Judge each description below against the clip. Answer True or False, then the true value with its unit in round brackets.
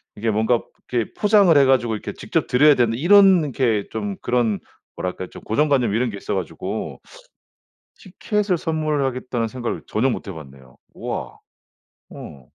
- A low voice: True (120 Hz)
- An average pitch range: False (6.0 semitones)